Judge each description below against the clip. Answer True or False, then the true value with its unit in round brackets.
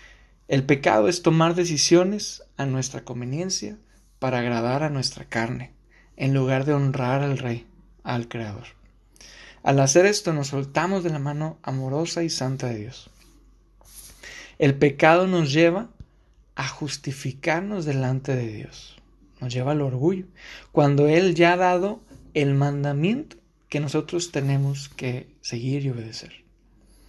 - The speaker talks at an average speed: True (135 wpm)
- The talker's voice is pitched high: False (140 Hz)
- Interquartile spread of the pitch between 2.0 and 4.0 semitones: False (4.6 semitones)